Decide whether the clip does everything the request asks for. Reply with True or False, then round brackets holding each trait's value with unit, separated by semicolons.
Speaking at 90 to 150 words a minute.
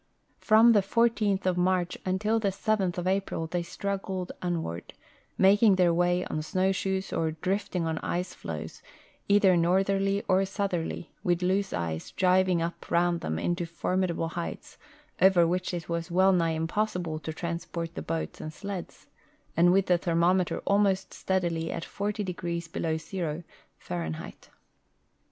True (145 wpm)